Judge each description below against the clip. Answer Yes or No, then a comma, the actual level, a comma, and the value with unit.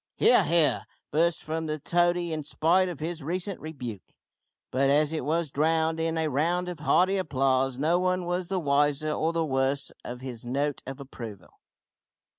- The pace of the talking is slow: No, average, 185 wpm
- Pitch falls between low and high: Yes, medium, 155 Hz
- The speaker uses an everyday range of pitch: Yes, average, 3.8 semitones